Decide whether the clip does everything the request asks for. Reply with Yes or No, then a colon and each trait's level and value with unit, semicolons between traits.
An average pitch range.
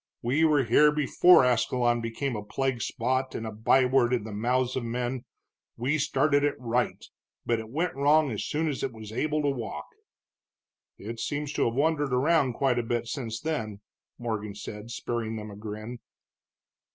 Yes: average, 3.8 semitones